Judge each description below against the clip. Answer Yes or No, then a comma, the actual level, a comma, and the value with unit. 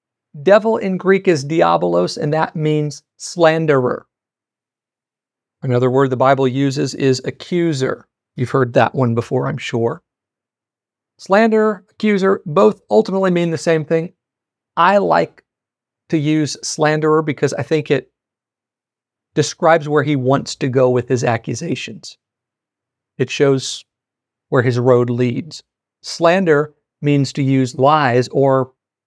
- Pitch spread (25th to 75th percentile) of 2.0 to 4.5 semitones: Yes, average, 4.0 semitones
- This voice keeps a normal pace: No, slow, 125 wpm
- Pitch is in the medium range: Yes, medium, 145 Hz